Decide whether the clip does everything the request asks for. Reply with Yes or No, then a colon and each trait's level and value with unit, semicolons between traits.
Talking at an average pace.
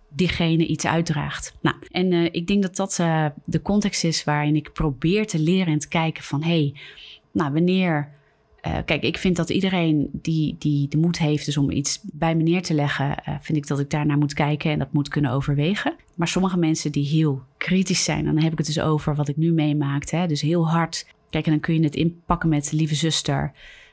No: fast, 225 wpm